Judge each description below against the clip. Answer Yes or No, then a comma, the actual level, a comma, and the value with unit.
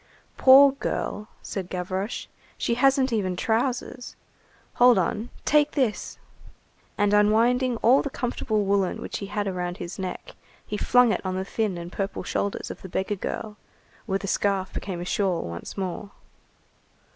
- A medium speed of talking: Yes, average, 155 wpm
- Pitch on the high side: Yes, high, 205 Hz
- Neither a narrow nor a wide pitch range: Yes, average, 4.4 semitones